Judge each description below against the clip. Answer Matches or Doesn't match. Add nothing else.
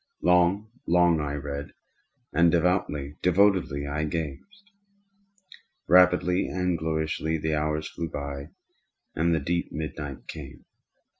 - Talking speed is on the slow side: Matches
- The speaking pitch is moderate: Doesn't match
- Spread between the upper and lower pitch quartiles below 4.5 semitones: Matches